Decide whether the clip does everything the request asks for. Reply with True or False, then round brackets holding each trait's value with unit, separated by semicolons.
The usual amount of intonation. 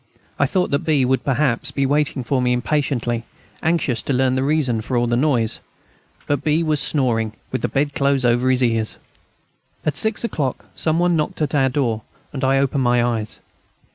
True (3.3 semitones)